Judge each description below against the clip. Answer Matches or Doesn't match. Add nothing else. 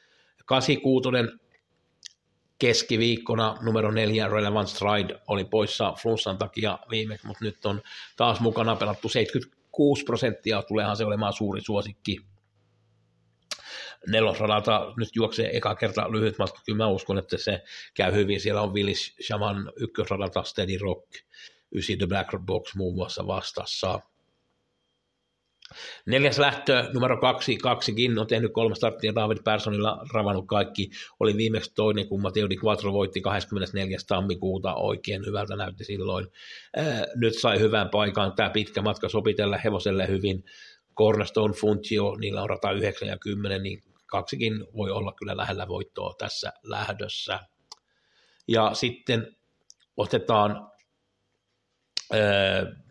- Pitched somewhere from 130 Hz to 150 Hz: Doesn't match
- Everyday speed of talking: Matches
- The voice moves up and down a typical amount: Doesn't match